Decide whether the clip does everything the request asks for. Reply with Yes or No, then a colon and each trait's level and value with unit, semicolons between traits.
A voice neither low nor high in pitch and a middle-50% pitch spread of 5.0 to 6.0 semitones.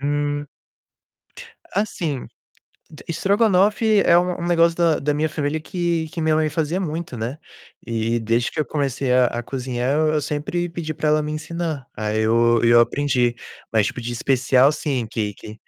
Yes: medium, 150 Hz; average, 5.3 semitones